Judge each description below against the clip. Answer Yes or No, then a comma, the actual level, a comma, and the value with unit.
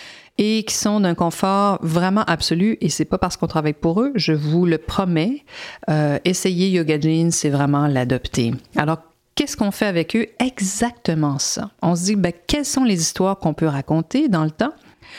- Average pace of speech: Yes, average, 190 wpm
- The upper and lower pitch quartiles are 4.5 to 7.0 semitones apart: Yes, average, 5.1 semitones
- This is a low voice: No, medium, 175 Hz